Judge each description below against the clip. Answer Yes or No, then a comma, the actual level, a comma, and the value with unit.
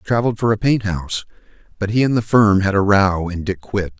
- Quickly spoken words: Yes, fast, 240 wpm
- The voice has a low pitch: Yes, low, 100 Hz